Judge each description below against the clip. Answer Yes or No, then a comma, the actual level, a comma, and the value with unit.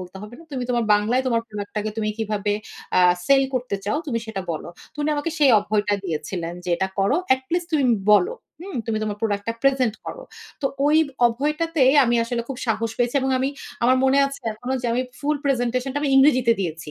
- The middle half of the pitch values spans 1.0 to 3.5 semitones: No, average, 4.6 semitones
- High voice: Yes, high, 240 Hz